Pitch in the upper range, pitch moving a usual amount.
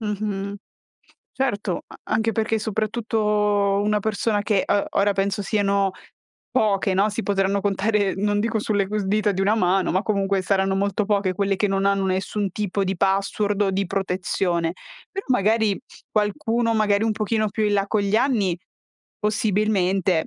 No: high, 205 Hz; narrow, 1.6 semitones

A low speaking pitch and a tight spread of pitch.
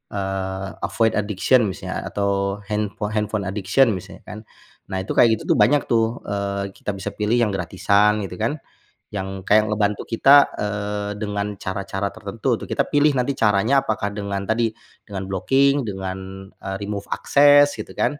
Yes: low, 105 Hz; narrow, 2.2 semitones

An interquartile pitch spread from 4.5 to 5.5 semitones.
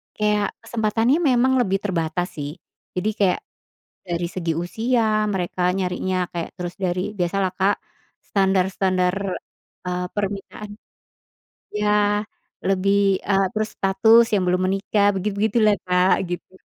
No: narrow, 2.6 semitones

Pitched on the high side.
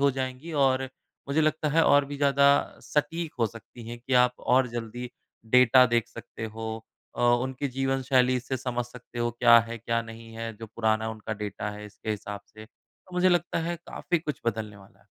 No: low, 120 Hz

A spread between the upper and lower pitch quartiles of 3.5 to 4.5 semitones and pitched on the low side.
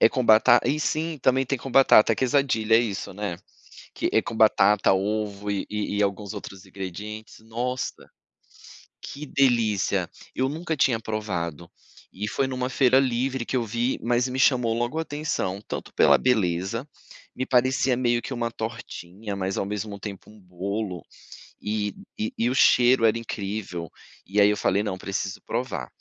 Yes: average, 3.9 semitones; low, 110 Hz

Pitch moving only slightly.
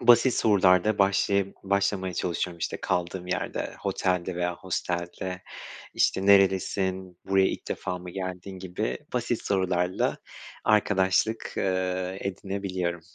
Yes: narrow, 1.5 semitones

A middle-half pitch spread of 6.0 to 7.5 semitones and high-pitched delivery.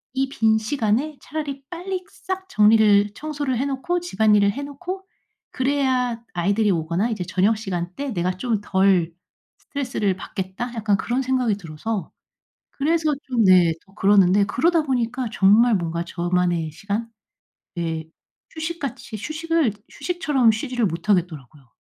Yes: wide, 6.7 semitones; high, 220 Hz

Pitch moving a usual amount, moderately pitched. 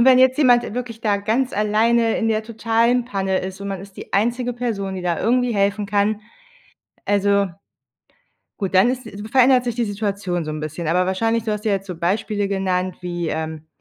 No: average, 3.5 semitones; high, 205 Hz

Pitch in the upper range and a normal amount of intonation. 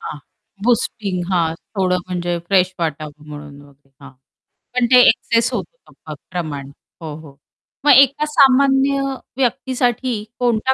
No: high, 195 Hz; wide, 8.7 semitones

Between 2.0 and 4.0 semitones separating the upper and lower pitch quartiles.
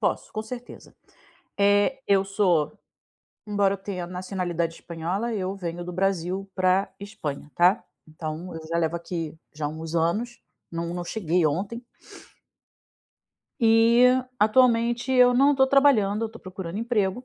No: average, 4.9 semitones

